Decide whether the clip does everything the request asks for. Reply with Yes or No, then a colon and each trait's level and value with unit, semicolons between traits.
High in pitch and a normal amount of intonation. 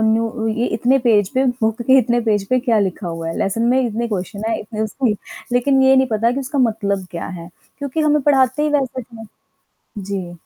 Yes: high, 230 Hz; average, 4.0 semitones